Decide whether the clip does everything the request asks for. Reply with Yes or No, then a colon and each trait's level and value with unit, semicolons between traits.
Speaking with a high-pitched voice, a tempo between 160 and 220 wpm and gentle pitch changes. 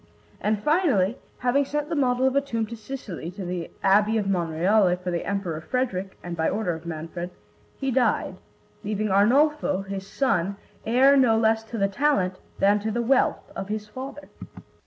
No: high, 210 Hz; average, 180 wpm; wide, 5.5 semitones